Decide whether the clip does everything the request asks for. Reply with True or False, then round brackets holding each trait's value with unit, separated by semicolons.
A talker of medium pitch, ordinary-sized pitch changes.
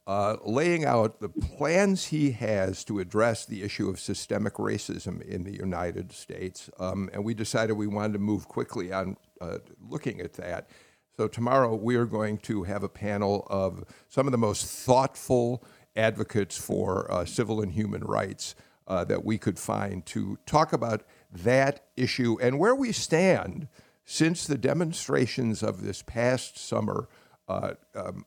False (110 Hz; 3.6 semitones)